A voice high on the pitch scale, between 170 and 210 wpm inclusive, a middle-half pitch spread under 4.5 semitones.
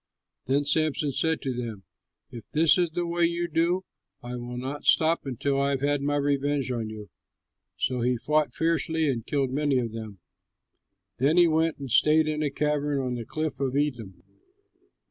No: medium, 145 Hz; average, 185 wpm; average, 3.9 semitones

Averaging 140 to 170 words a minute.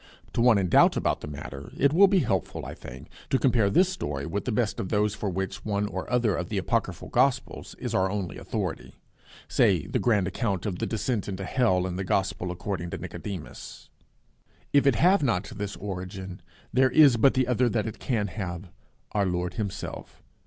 No: average, 200 wpm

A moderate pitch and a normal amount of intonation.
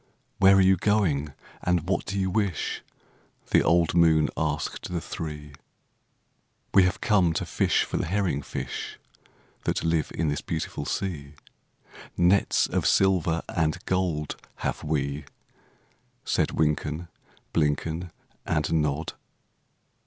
No: very low, 80 Hz; average, 3.5 semitones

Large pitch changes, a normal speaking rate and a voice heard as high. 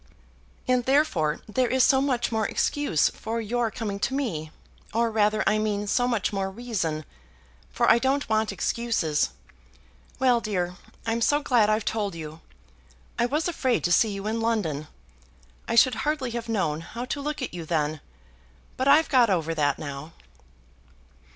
Yes: wide, 5.8 semitones; average, 165 wpm; high, 220 Hz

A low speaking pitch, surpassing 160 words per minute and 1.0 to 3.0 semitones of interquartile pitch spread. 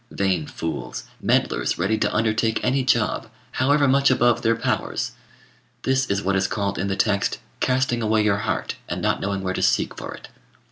No: low, 110 Hz; average, 185 wpm; average, 4.3 semitones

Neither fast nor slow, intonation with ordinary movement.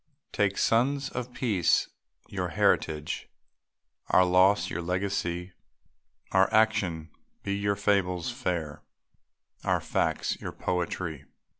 No: slow, 105 wpm; average, 3.1 semitones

